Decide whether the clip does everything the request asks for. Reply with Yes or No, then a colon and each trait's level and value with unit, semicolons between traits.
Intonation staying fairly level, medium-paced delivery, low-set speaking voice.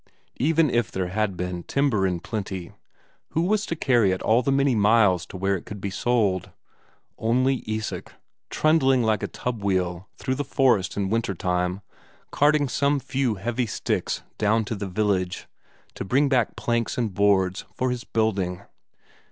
No: average, 5.1 semitones; average, 170 wpm; low, 110 Hz